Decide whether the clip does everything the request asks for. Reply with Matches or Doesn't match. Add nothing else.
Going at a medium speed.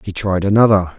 Matches